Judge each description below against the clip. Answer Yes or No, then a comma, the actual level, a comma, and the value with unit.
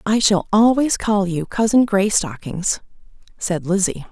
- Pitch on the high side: Yes, high, 195 Hz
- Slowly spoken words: Yes, slow, 130 wpm